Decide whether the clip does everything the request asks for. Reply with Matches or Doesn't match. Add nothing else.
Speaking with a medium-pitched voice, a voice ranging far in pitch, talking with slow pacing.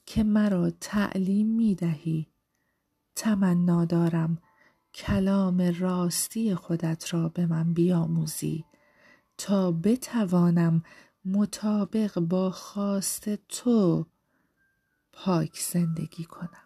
Doesn't match